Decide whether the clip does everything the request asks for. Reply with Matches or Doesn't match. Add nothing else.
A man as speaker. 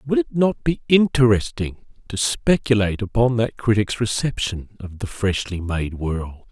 Matches